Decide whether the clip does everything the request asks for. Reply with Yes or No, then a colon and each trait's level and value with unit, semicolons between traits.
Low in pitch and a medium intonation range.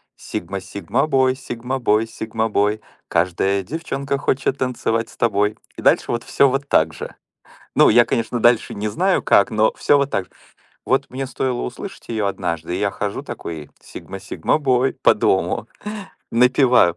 Yes: low, 115 Hz; average, 4.6 semitones